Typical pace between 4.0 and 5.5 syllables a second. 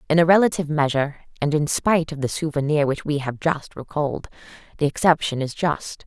No: 6.1 syllables/s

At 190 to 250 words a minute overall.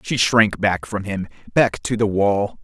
Yes: fast, 205 wpm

